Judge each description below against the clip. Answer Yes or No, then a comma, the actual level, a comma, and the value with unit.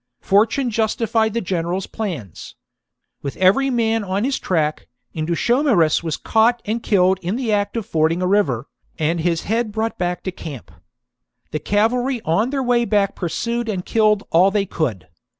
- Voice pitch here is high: Yes, high, 205 Hz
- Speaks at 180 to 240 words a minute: No, average, 165 wpm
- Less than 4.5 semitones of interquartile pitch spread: No, average, 4.9 semitones